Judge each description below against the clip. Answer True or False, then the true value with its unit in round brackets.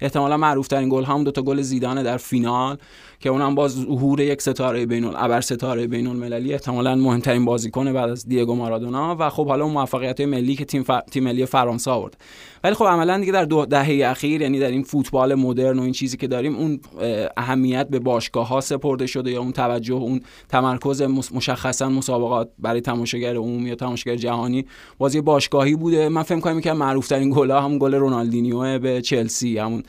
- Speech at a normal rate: False (195 wpm)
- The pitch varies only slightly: True (2.2 semitones)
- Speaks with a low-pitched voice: True (130 Hz)